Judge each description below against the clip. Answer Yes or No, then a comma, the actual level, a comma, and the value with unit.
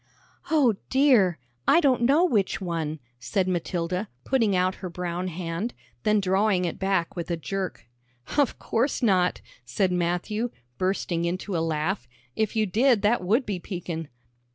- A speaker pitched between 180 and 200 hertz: Yes, medium, 185 Hz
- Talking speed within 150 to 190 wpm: Yes, average, 155 wpm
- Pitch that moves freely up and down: No, average, 4.1 semitones